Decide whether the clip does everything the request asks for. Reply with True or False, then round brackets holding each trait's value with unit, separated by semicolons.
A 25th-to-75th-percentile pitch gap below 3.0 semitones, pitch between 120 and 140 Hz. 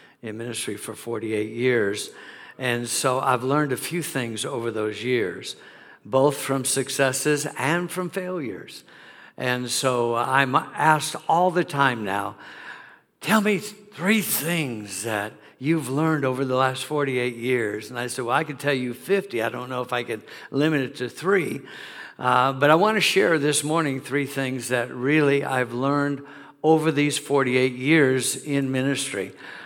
False (3.3 semitones; 135 Hz)